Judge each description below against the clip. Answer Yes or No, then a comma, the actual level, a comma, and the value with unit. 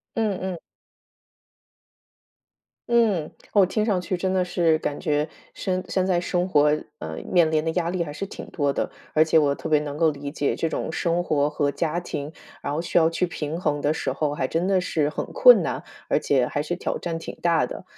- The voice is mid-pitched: Yes, medium, 165 Hz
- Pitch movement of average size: Yes, average, 3.4 semitones